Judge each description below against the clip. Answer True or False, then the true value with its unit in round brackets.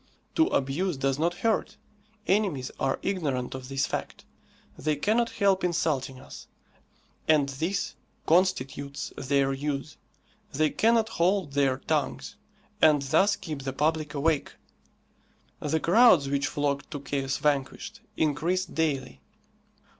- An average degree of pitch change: True (4.9 semitones)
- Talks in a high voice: False (150 Hz)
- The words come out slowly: True (125 wpm)